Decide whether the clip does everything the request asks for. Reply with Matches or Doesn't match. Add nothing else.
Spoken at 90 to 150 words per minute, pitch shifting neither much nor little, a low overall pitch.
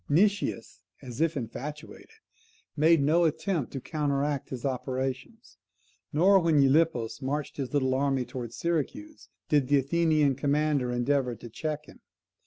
Doesn't match